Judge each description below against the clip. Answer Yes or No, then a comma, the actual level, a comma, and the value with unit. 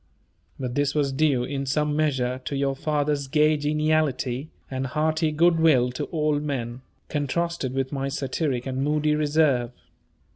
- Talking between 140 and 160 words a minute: Yes, average, 150 wpm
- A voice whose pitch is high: No, medium, 145 Hz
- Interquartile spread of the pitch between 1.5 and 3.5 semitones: Yes, narrow, 2.5 semitones